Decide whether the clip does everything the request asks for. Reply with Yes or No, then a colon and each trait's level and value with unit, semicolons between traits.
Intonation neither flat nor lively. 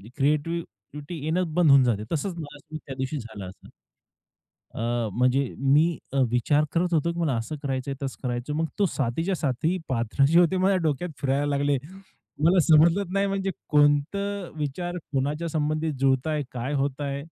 Yes: average, 3.8 semitones